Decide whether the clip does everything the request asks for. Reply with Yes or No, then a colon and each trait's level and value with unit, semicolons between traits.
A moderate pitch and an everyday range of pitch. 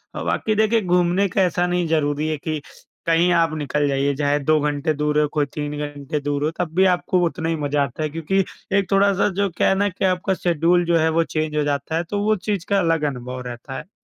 Yes: medium, 160 Hz; average, 3.5 semitones